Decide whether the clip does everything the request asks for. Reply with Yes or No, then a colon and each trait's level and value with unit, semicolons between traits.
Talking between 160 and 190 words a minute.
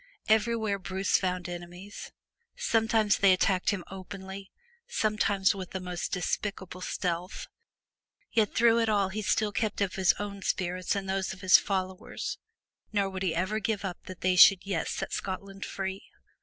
Yes: average, 165 wpm